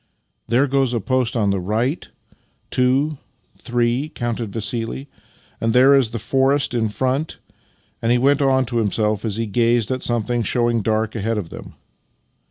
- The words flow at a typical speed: Yes, average, 180 wpm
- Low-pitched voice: Yes, low, 120 Hz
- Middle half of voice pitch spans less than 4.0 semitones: Yes, average, 2.8 semitones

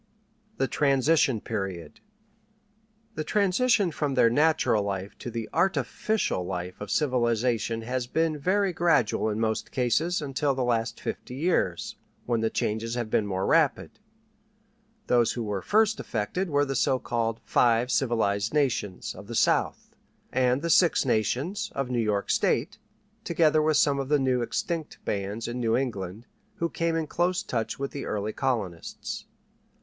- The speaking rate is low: No, average, 155 wpm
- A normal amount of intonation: No, wide, 5.7 semitones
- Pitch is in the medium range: No, low, 125 Hz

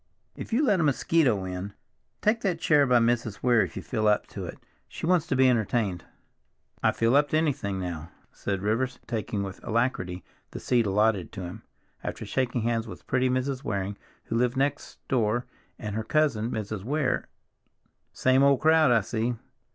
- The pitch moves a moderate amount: Yes, average, 4.7 semitones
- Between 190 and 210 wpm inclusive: No, average, 175 wpm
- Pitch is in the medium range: No, low, 120 Hz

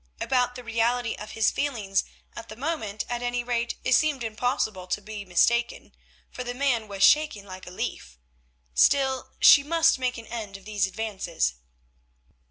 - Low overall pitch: No, high, 230 Hz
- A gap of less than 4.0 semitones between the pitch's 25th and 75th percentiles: Yes, average, 3.6 semitones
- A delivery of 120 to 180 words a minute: Yes, average, 170 wpm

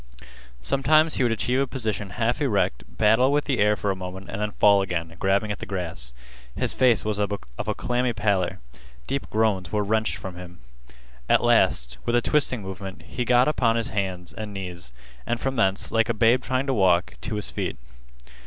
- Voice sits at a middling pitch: No, low, 105 Hz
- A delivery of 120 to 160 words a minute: No, average, 200 wpm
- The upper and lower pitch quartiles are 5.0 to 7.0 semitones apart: No, average, 4.3 semitones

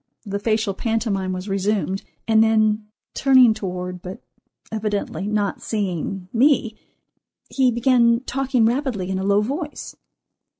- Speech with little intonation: No, average, 3.3 semitones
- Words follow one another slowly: Yes, slow, 125 wpm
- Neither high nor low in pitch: No, high, 215 Hz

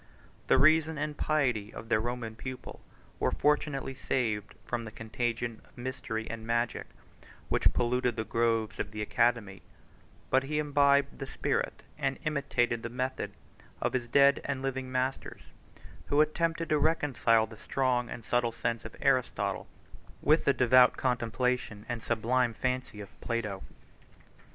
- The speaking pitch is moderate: No, low, 125 Hz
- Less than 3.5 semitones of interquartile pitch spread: Yes, average, 3.1 semitones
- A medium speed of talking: Yes, average, 145 wpm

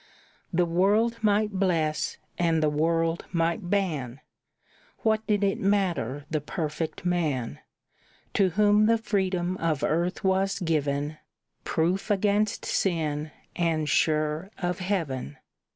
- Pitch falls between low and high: Yes, medium, 175 Hz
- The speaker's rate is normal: No, slow, 120 wpm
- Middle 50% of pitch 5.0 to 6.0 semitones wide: No, average, 4.1 semitones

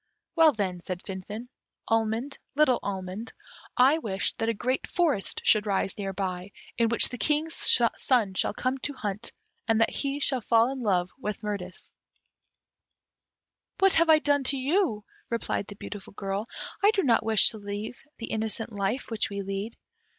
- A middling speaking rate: Yes, average, 170 wpm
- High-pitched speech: Yes, high, 225 Hz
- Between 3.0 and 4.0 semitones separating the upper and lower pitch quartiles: No, average, 4.7 semitones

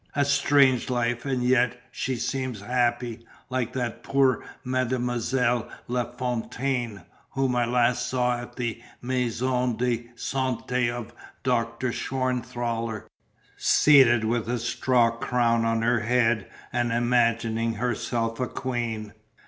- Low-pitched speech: Yes, low, 120 Hz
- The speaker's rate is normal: No, slow, 120 wpm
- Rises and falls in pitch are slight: Yes, narrow, 1.5 semitones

